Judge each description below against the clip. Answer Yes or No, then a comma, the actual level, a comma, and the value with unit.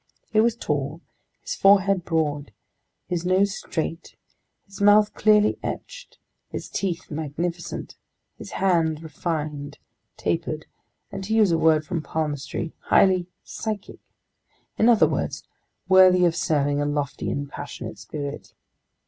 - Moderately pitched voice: Yes, medium, 170 Hz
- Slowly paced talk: Yes, slow, 125 wpm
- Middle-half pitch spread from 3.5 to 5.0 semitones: Yes, average, 4.4 semitones